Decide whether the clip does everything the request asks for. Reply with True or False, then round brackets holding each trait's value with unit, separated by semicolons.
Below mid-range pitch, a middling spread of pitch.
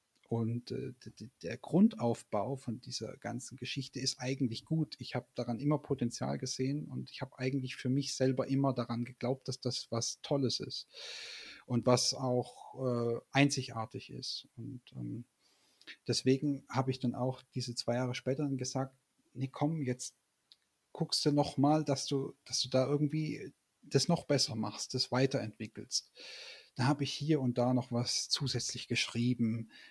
False (130 Hz; 2.3 semitones)